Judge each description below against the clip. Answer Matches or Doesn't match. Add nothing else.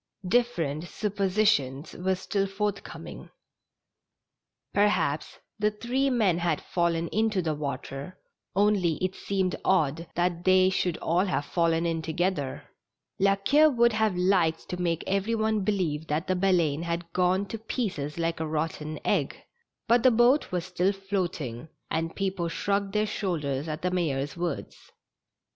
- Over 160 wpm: Doesn't match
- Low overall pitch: Doesn't match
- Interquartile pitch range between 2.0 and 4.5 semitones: Matches